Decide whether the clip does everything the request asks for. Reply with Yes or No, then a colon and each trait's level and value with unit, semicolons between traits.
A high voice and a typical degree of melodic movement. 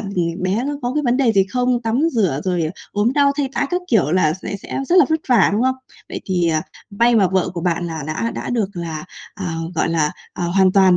No: high, 195 Hz; wide, 6.0 semitones